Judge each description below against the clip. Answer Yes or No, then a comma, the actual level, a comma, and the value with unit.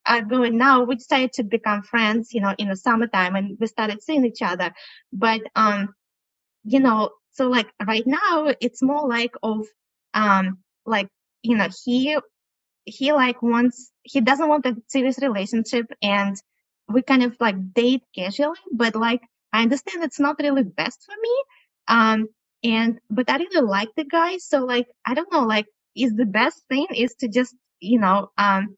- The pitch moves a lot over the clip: No, average, 3.8 semitones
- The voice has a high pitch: Yes, high, 240 Hz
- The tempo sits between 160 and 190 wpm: Yes, average, 180 wpm